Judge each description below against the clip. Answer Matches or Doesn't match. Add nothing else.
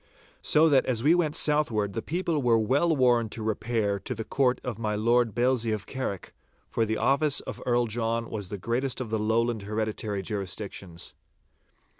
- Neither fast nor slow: Matches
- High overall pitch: Doesn't match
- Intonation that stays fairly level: Doesn't match